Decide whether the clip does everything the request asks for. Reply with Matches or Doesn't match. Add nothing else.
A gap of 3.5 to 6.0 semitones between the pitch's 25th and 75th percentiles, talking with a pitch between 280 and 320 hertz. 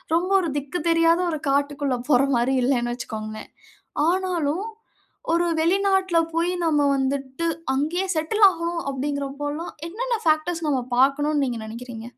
Matches